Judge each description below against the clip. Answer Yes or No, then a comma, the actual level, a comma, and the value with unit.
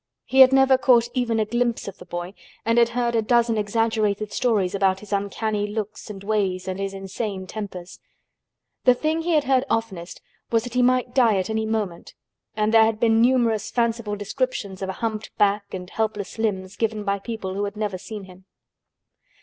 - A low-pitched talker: No, high, 215 Hz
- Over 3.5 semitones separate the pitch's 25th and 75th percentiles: No, average, 2.8 semitones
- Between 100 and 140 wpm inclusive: No, average, 195 wpm